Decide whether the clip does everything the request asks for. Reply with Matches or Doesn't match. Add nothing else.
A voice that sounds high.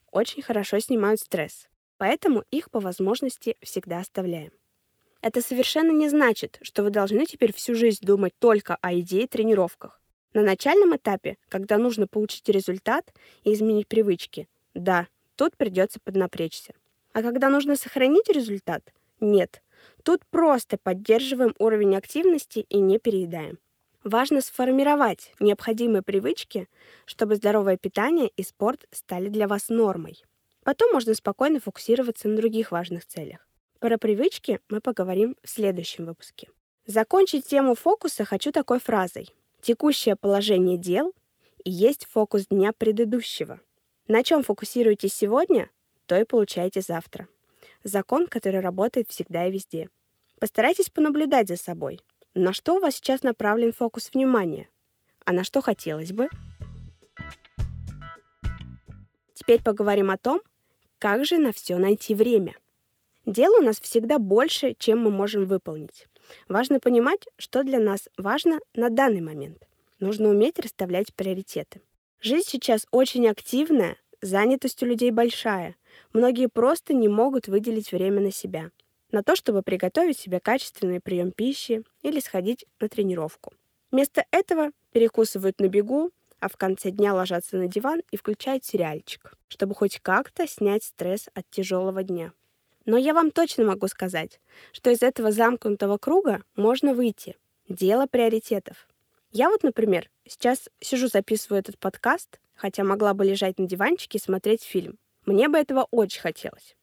Matches